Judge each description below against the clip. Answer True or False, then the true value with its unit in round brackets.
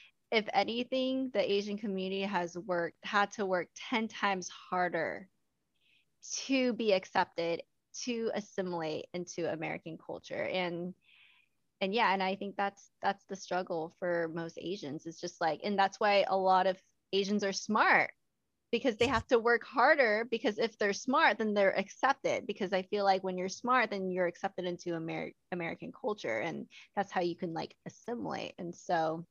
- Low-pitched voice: False (195 Hz)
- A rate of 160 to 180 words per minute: True (170 wpm)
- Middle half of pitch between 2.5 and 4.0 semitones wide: True (3.5 semitones)